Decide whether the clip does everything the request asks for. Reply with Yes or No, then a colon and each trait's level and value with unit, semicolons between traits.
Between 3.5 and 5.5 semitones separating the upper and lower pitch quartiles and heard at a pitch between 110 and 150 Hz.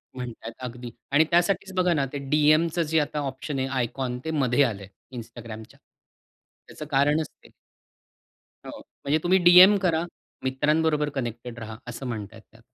Yes: average, 4.7 semitones; medium, 140 Hz